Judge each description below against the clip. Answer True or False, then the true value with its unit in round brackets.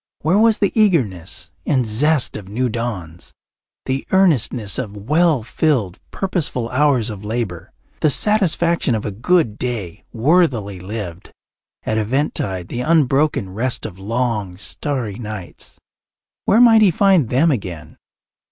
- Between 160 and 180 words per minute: False (135 wpm)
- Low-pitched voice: True (120 Hz)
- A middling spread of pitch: False (7.1 semitones)